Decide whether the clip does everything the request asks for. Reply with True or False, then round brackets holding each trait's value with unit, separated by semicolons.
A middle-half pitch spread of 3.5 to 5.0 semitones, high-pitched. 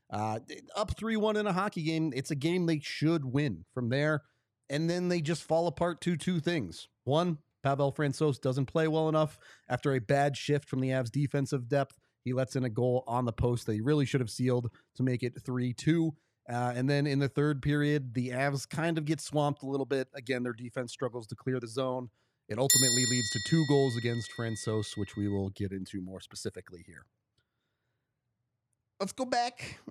False (3.8 semitones; 135 Hz)